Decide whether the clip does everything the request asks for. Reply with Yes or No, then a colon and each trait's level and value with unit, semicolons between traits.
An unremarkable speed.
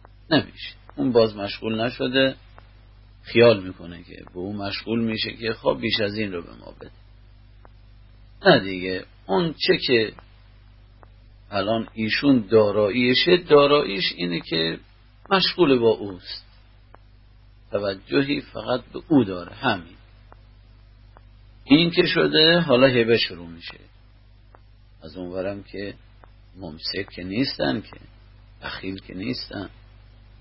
Yes: average, 115 wpm